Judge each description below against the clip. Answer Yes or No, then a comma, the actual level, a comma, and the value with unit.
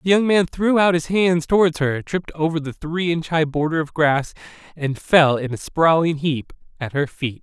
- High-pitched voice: No, medium, 160 Hz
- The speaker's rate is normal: No, fast, 220 wpm